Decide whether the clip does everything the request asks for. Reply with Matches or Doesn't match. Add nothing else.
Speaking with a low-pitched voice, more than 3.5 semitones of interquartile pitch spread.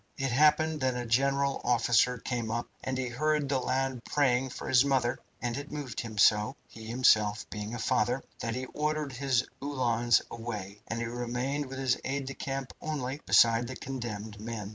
Doesn't match